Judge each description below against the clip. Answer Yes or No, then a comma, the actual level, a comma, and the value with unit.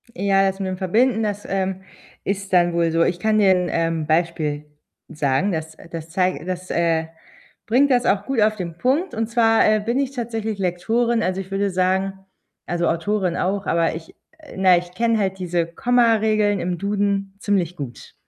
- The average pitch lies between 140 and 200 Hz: Yes, high, 190 Hz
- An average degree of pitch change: Yes, average, 3.8 semitones